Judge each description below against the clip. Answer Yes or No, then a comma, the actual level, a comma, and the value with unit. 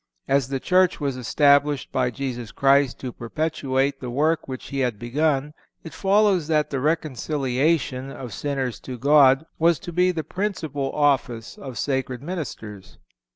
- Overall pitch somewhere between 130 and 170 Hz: Yes, medium, 140 Hz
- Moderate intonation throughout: Yes, average, 3.3 semitones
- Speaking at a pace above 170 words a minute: No, average, 155 wpm